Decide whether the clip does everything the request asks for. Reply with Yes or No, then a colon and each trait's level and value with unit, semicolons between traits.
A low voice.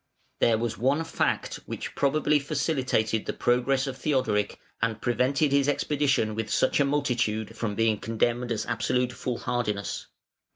Yes: low, 125 Hz